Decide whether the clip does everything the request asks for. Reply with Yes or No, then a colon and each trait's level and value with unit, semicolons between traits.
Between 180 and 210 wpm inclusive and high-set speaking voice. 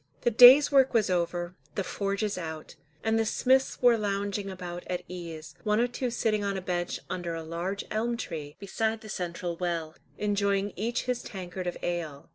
Yes: average, 185 wpm; high, 195 Hz